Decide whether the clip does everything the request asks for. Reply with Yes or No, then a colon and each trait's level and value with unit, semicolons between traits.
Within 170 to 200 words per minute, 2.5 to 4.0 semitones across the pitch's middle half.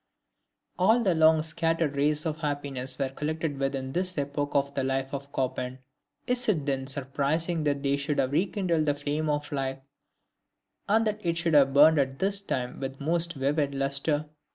Yes: average, 180 wpm; average, 3.1 semitones